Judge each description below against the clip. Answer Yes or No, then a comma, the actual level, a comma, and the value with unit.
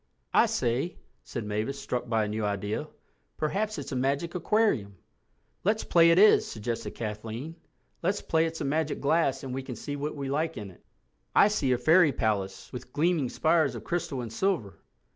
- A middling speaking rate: Yes, average, 180 wpm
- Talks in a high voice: No, medium, 140 Hz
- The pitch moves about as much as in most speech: No, wide, 6.4 semitones